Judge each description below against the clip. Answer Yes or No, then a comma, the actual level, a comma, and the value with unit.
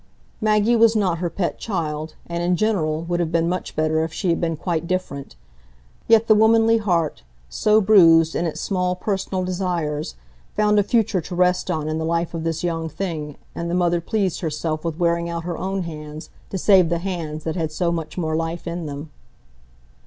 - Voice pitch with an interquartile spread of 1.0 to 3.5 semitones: Yes, average, 2.8 semitones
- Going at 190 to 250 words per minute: Yes, average, 200 wpm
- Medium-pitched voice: Yes, medium, 170 Hz